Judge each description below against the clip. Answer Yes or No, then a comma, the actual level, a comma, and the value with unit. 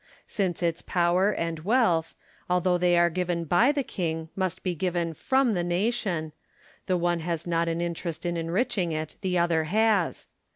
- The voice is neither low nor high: Yes, medium, 175 Hz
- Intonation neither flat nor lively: No, narrow, 2.1 semitones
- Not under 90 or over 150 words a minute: No, average, 175 wpm